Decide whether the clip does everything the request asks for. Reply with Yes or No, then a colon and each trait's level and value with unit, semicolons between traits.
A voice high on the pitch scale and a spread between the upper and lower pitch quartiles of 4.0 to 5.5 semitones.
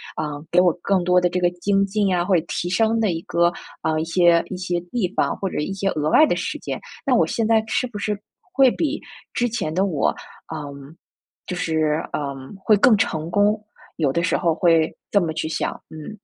No: medium, 180 Hz; average, 4.3 semitones